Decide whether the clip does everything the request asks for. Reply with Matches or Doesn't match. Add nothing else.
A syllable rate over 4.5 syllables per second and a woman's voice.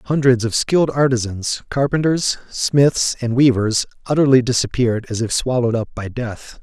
Doesn't match